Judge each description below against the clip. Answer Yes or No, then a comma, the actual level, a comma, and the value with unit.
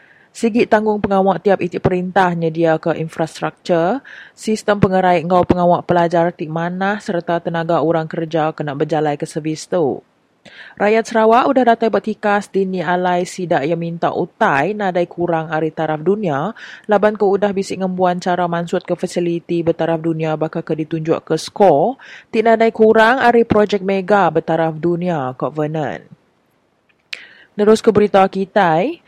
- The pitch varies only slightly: No, average, 3.8 semitones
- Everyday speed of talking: Yes, average, 145 wpm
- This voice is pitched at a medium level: Yes, medium, 180 Hz